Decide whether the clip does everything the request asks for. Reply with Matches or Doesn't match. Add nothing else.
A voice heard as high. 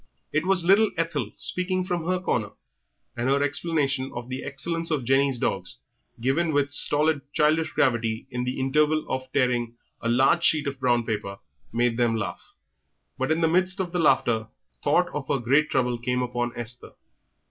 Doesn't match